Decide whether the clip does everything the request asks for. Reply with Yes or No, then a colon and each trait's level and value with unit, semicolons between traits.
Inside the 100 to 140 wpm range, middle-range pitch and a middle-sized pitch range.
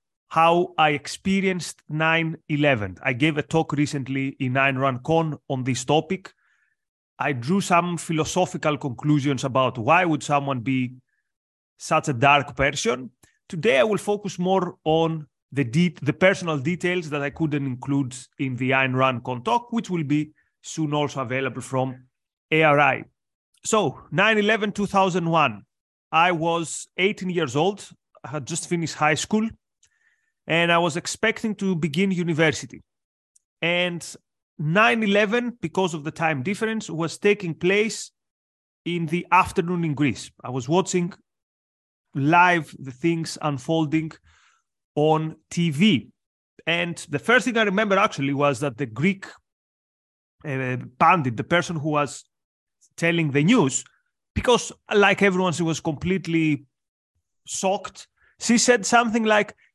Yes: slow, 135 wpm; medium, 160 Hz; average, 4.6 semitones